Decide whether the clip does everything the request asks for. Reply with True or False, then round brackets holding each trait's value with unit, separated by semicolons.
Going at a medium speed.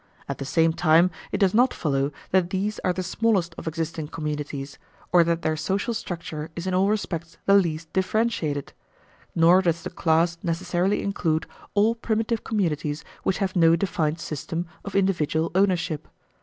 True (165 wpm)